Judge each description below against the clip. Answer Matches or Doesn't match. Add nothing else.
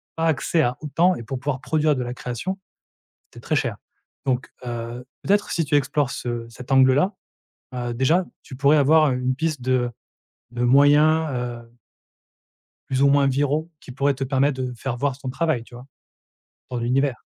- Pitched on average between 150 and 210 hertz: Doesn't match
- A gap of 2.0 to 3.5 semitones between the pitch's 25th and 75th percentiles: Matches